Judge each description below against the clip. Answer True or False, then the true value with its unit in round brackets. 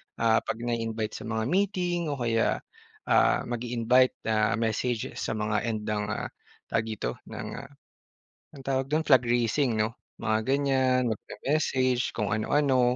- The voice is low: True (120 Hz)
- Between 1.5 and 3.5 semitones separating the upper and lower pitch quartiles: True (3.1 semitones)